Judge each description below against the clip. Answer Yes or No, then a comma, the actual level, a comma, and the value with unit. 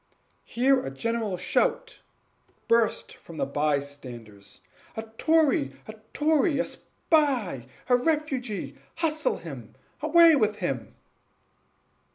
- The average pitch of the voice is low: No, high, 230 Hz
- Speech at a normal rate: No, slow, 105 wpm